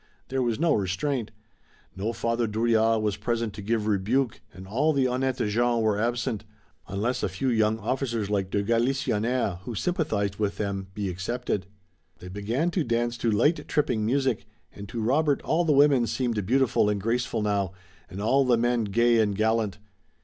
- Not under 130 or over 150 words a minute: No, average, 175 wpm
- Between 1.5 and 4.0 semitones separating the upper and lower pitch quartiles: Yes, average, 3.5 semitones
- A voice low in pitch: Yes, low, 115 Hz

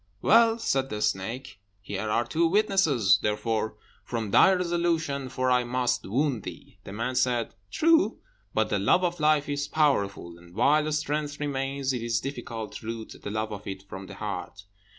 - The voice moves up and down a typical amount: No, wide, 5.9 semitones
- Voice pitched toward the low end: Yes, low, 125 Hz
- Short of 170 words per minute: No, average, 175 wpm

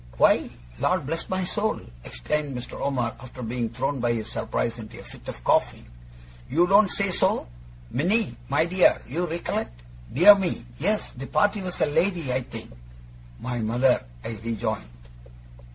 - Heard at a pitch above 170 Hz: No, medium, 140 Hz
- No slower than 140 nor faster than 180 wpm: Yes, average, 160 wpm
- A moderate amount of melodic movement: No, wide, 7.1 semitones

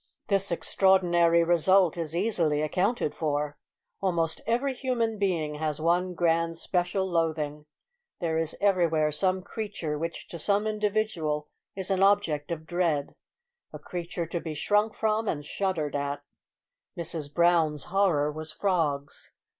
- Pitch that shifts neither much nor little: Yes, average, 3.9 semitones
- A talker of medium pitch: Yes, medium, 170 Hz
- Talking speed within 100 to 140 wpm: Yes, slow, 135 wpm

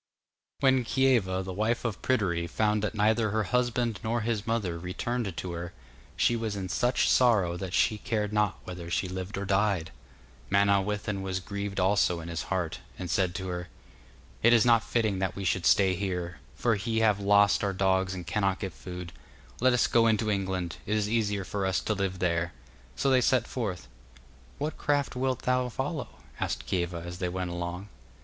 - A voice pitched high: No, low, 100 Hz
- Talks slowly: No, average, 190 wpm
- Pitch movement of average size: Yes, average, 3.6 semitones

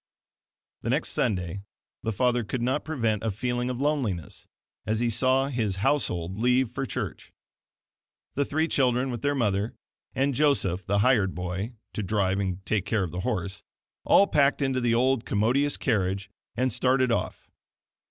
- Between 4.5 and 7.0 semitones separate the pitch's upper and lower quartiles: Yes, average, 4.9 semitones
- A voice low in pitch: Yes, low, 120 Hz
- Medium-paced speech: Yes, average, 160 wpm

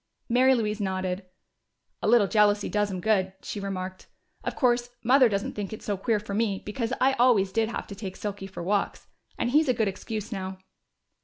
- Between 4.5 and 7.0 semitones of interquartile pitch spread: No, average, 3.1 semitones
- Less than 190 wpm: No, average, 200 wpm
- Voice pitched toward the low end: No, high, 210 Hz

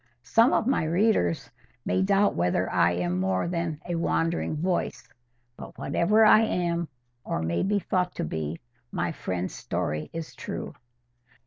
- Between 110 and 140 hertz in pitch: No, medium, 165 Hz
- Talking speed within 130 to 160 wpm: Yes, average, 150 wpm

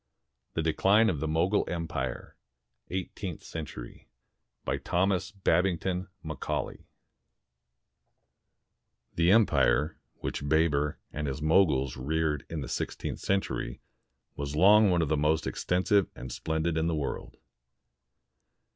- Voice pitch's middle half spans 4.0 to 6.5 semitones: No, average, 3.6 semitones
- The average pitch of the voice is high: No, very low, 80 Hz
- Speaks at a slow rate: Yes, slow, 115 wpm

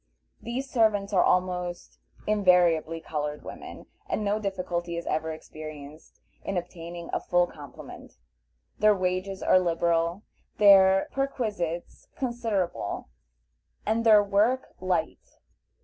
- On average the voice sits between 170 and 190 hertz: Yes, medium, 185 Hz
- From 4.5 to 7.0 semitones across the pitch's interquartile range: No, average, 3.7 semitones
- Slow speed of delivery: Yes, slow, 110 wpm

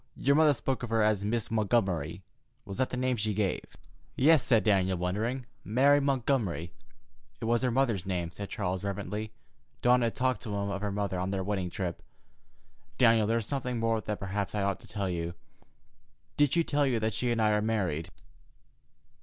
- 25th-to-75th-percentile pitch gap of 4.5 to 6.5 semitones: No, average, 4.1 semitones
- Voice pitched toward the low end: Yes, low, 110 Hz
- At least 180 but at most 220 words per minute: Yes, average, 195 wpm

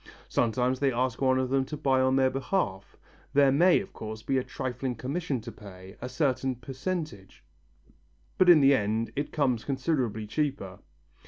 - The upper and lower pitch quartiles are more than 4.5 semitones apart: No, average, 3.5 semitones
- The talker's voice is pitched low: Yes, low, 130 Hz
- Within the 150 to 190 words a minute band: Yes, average, 170 wpm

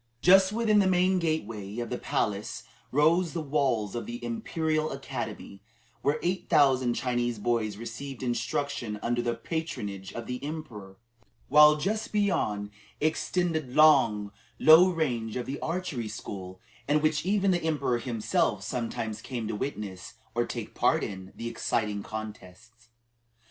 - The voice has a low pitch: Yes, low, 125 Hz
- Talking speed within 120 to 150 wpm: Yes, average, 145 wpm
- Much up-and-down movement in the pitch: Yes, wide, 6.2 semitones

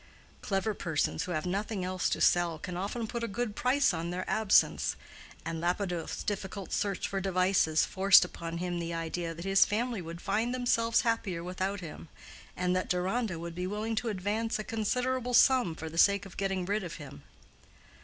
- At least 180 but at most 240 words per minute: Yes, average, 185 wpm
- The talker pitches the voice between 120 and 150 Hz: No, high, 190 Hz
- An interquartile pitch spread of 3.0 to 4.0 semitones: Yes, average, 3.7 semitones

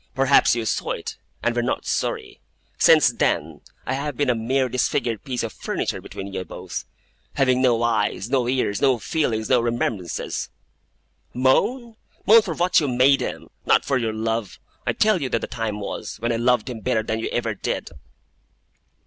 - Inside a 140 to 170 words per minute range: No, average, 185 wpm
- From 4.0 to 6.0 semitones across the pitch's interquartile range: No, average, 3.0 semitones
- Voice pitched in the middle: No, low, 120 Hz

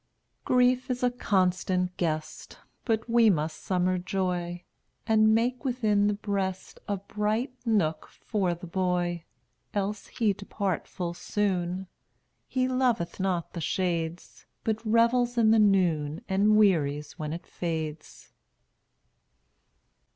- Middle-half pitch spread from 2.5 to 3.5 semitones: No, average, 4.0 semitones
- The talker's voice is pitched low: No, high, 195 Hz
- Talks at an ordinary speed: No, slow, 125 wpm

